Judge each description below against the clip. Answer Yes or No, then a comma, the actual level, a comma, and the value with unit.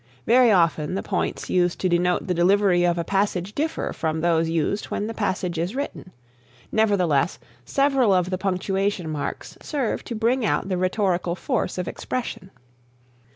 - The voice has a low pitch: No, medium, 185 Hz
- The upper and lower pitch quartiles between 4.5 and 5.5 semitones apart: No, average, 3.2 semitones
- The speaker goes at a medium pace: Yes, average, 160 wpm